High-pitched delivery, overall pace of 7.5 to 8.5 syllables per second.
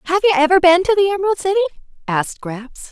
Yes: very high, 345 Hz; 8.1 syllables/s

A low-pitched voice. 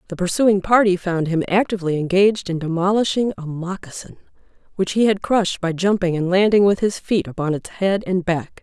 No: medium, 185 Hz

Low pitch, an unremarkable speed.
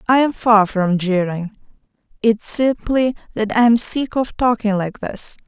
No: high, 220 Hz; average, 155 wpm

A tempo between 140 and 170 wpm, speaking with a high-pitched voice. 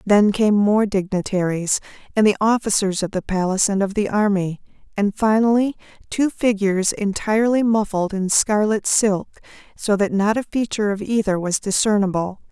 Yes: average, 155 wpm; high, 205 Hz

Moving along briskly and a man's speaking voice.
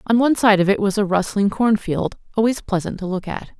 No: fast, 235 wpm; female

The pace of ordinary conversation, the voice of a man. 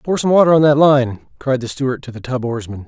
No: fast, 270 wpm; male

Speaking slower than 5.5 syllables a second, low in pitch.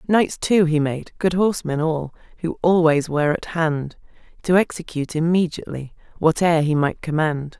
No: 5.2 syllables/s; medium, 160 Hz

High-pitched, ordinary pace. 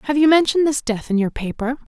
No: very high, 265 Hz; fast, 245 wpm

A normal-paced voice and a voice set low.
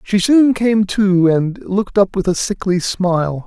No: average, 190 wpm; high, 195 Hz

